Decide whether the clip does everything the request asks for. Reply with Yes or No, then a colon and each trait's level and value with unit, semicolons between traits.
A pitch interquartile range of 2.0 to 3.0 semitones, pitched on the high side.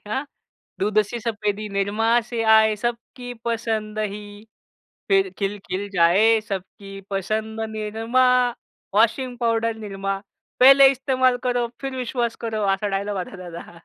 Yes: average, 2.7 semitones; high, 220 Hz